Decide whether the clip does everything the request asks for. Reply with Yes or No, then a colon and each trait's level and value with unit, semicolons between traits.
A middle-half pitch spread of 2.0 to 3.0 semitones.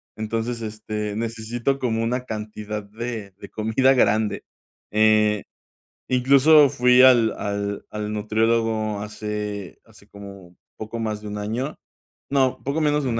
Yes: narrow, 2.6 semitones